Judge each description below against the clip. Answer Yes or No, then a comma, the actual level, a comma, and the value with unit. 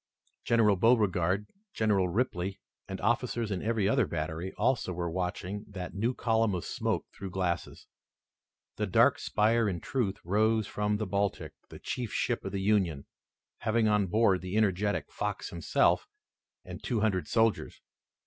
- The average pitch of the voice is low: Yes, low, 105 Hz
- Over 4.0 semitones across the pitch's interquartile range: No, average, 3.2 semitones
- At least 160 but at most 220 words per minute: No, average, 150 wpm